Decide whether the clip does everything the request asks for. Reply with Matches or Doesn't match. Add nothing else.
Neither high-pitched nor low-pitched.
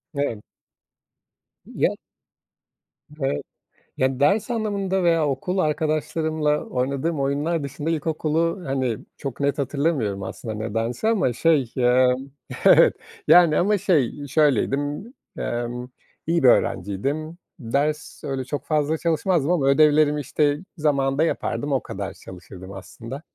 Matches